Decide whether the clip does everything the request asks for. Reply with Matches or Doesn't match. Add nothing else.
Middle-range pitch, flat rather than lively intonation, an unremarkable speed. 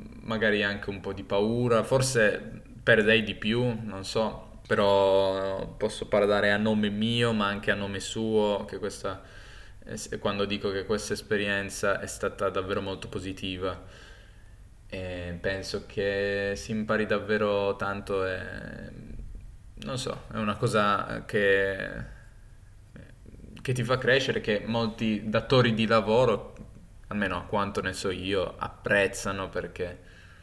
Doesn't match